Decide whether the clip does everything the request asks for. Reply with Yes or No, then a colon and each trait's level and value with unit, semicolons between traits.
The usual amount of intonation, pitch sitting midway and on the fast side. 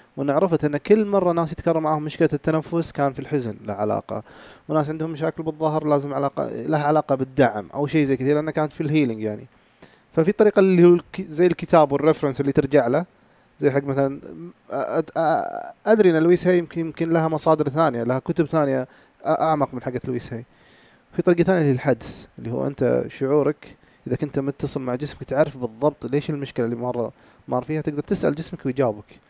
Yes: average, 3.2 semitones; medium, 150 Hz; fast, 180 wpm